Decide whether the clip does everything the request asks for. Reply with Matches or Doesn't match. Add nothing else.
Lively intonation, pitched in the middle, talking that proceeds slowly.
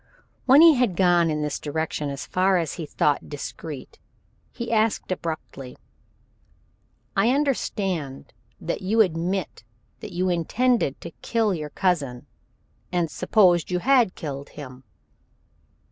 Matches